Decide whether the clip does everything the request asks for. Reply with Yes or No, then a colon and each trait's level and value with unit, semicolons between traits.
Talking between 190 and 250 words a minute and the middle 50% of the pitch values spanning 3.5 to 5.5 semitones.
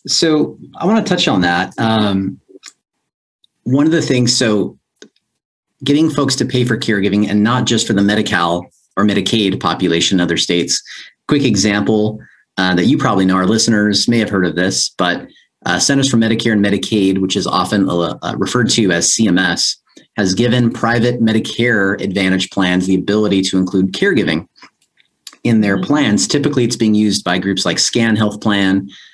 No: average, 170 wpm; average, 3.8 semitones